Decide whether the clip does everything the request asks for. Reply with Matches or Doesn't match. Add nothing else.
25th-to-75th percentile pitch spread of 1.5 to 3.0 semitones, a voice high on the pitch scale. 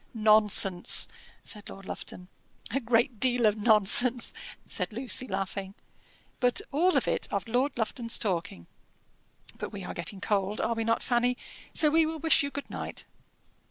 Doesn't match